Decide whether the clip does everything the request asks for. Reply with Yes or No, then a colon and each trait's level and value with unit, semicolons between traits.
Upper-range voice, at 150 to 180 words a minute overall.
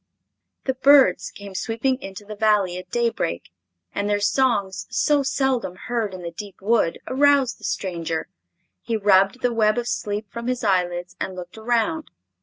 Yes: high, 210 Hz; average, 165 wpm